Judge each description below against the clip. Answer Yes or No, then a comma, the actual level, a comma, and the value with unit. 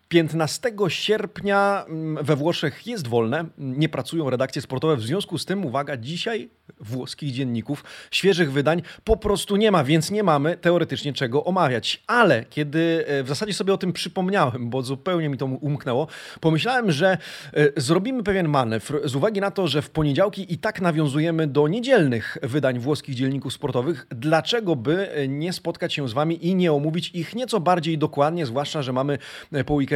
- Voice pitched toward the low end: No, medium, 155 Hz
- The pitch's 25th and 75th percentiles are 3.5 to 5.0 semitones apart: Yes, average, 4.2 semitones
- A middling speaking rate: No, fast, 165 wpm